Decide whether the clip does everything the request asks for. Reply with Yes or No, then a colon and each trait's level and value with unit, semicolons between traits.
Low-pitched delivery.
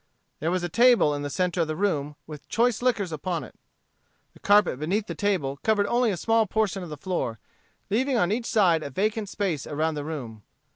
No: medium, 185 Hz